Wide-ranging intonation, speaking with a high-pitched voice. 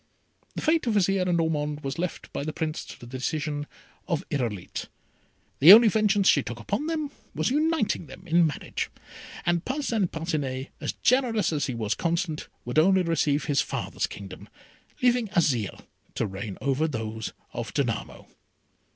No: wide, 6.8 semitones; medium, 160 Hz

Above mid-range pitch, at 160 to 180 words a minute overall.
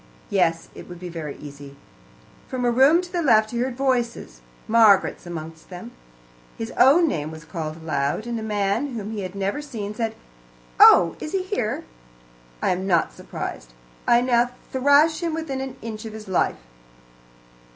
Yes: high, 220 Hz; average, 170 wpm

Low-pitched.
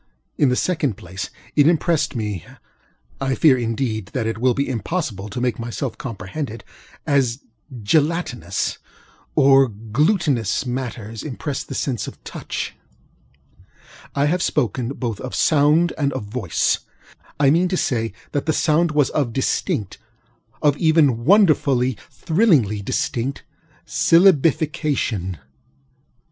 Yes: low, 130 Hz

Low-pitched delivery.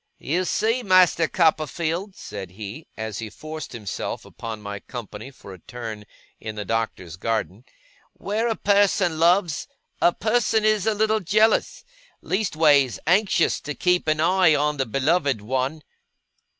No: medium, 155 Hz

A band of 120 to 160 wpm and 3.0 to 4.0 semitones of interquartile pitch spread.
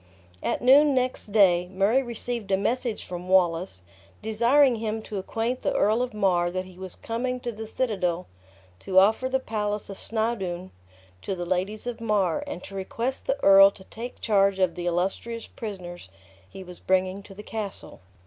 No: average, 175 wpm; average, 3.7 semitones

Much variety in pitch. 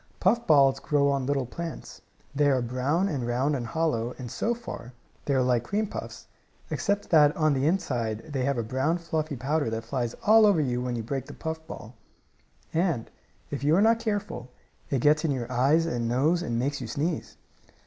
No: average, 4.6 semitones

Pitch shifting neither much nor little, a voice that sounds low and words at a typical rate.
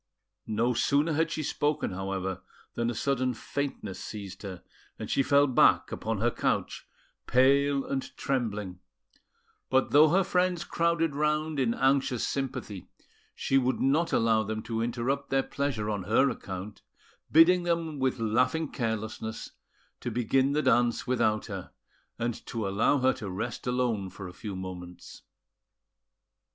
Yes: average, 4.7 semitones; low, 125 Hz; average, 145 wpm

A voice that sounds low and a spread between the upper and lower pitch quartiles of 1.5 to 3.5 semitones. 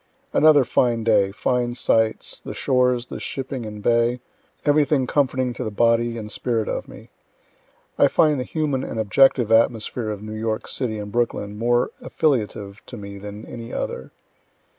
Yes: low, 115 Hz; average, 2.8 semitones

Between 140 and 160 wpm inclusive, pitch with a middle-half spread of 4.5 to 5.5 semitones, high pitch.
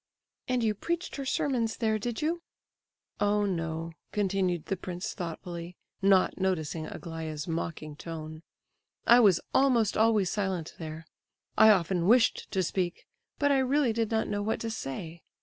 Yes: average, 150 wpm; average, 5.1 semitones; high, 195 Hz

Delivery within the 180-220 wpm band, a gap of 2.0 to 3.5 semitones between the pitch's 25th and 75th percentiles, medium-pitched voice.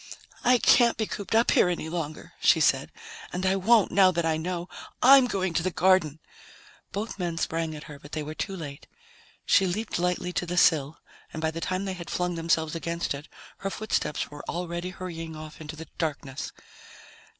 Yes: average, 195 wpm; average, 3.0 semitones; medium, 170 Hz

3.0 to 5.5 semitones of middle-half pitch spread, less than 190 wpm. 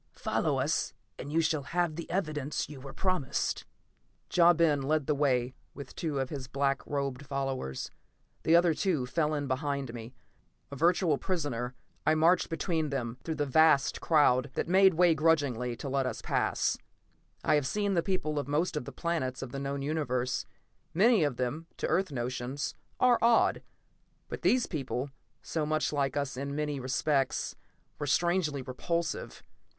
Yes: average, 3.6 semitones; average, 170 wpm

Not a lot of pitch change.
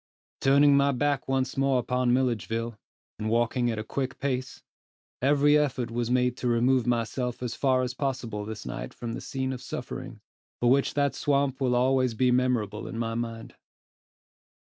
Yes: narrow, 2.3 semitones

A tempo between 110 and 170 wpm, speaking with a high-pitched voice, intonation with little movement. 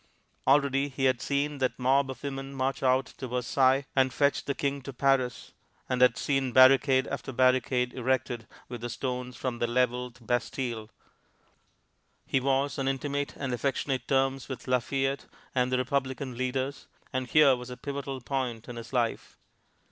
No: average, 165 wpm; low, 130 Hz; narrow, 1.5 semitones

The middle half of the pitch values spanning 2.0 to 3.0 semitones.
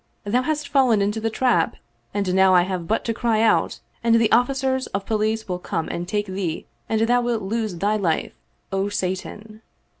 No: average, 3.4 semitones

